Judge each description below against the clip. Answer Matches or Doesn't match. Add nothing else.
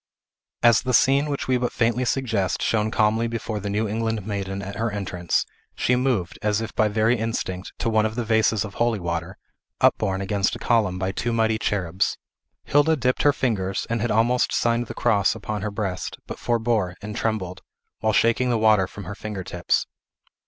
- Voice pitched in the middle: Doesn't match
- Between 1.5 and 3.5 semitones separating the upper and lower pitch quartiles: Matches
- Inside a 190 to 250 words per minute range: Matches